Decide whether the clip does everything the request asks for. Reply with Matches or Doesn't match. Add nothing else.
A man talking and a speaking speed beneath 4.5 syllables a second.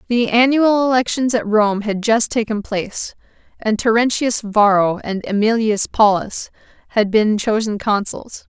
Doesn't match